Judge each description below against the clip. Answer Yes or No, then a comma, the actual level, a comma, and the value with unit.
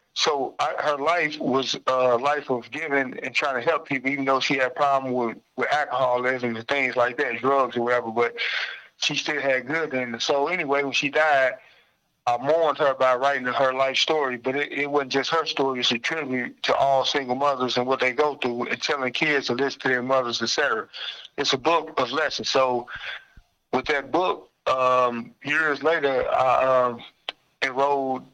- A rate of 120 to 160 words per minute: No, average, 195 wpm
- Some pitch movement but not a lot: No, narrow, 2.2 semitones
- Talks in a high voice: No, low, 135 Hz